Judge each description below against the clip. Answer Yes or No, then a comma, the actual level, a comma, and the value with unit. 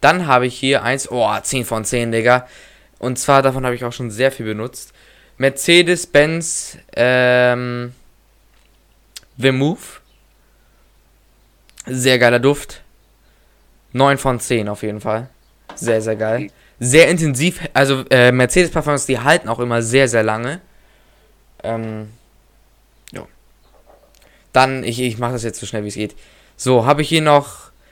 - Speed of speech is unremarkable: Yes, average, 140 wpm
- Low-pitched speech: Yes, low, 125 Hz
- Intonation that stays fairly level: No, average, 3.1 semitones